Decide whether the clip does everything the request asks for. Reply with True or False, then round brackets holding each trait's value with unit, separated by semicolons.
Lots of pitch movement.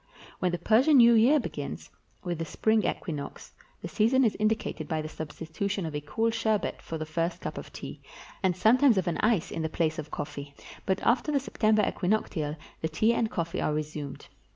True (5.9 semitones)